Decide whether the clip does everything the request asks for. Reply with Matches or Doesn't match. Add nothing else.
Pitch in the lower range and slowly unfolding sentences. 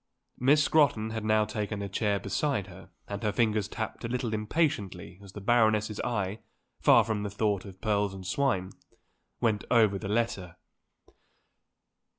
Doesn't match